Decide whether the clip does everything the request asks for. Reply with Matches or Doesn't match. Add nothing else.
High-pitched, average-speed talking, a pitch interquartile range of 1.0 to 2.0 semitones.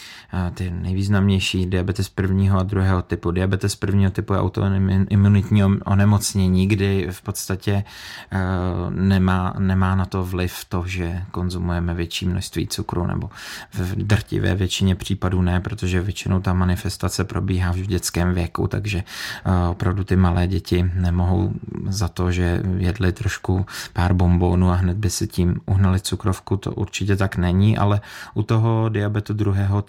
Doesn't match